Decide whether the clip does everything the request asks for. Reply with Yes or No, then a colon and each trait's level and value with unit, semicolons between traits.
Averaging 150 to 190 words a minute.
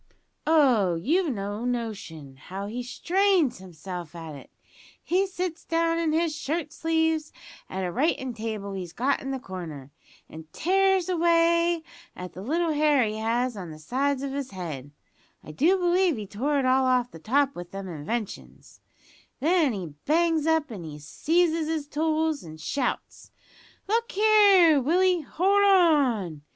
Yes: average, 155 wpm